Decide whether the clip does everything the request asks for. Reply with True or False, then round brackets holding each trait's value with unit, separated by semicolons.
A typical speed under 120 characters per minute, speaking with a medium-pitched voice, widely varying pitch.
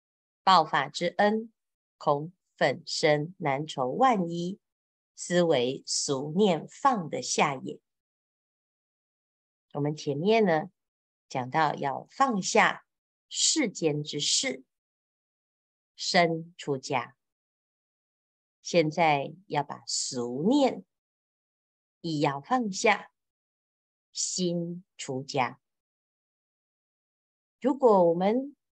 True (110 characters per minute; 170 Hz; 6.7 semitones)